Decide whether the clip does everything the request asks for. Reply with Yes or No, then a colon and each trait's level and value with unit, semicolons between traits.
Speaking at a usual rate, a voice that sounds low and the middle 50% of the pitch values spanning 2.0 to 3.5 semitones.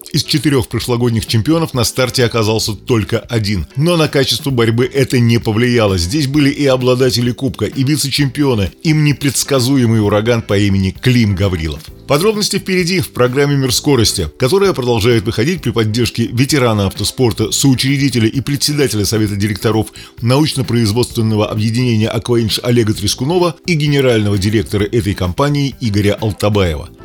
No: average, 135 wpm; low, 120 Hz; average, 4.2 semitones